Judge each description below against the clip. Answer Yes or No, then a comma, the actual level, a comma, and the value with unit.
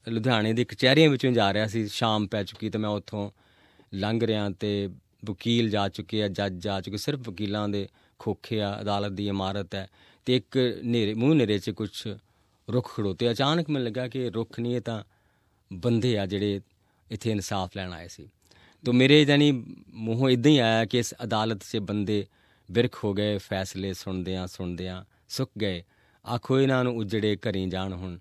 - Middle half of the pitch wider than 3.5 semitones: No, average, 3.2 semitones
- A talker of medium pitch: No, low, 105 Hz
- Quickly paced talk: Yes, fast, 180 wpm